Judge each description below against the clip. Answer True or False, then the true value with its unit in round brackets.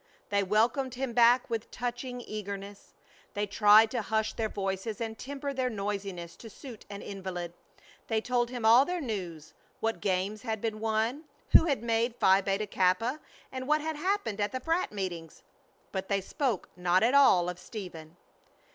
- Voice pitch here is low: False (220 Hz)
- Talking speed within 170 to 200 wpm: True (175 wpm)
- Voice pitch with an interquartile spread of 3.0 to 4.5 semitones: True (4.1 semitones)